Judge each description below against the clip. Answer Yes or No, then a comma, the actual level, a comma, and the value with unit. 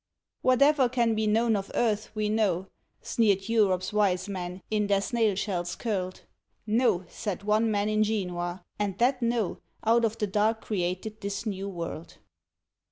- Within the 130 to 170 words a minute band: Yes, average, 160 wpm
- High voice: Yes, high, 210 Hz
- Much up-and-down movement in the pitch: No, average, 2.8 semitones